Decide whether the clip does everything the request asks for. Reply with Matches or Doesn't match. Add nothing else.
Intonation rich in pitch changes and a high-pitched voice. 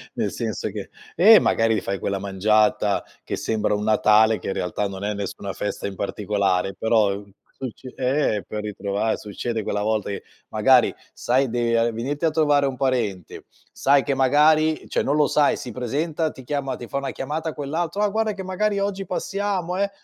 Doesn't match